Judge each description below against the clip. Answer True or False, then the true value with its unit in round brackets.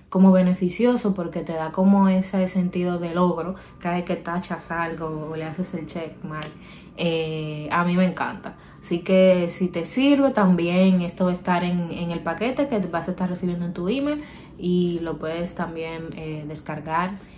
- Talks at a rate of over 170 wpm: True (185 wpm)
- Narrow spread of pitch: True (1.9 semitones)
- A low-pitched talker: False (175 Hz)